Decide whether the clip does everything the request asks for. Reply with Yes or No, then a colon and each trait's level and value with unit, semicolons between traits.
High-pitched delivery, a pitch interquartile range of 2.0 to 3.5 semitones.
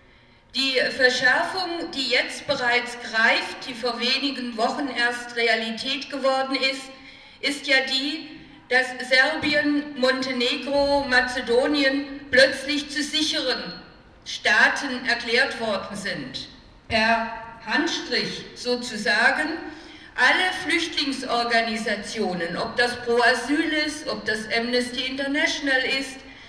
Yes: very high, 260 Hz; average, 3.1 semitones